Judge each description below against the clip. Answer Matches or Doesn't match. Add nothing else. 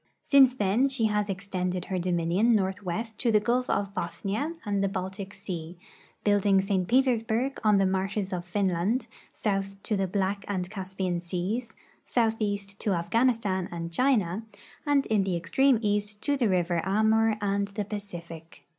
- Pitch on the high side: Matches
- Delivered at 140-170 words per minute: Matches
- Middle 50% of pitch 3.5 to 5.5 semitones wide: Doesn't match